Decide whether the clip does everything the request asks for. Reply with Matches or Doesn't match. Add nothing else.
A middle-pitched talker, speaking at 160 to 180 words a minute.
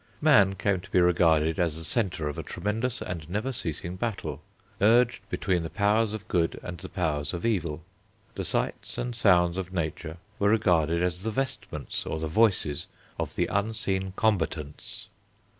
Doesn't match